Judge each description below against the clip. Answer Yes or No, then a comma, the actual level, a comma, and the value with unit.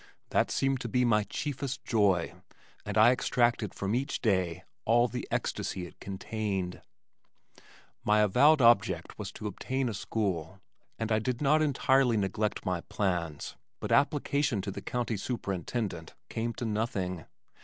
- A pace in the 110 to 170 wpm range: Yes, average, 145 wpm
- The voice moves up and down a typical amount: Yes, average, 4.3 semitones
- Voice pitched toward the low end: Yes, low, 110 Hz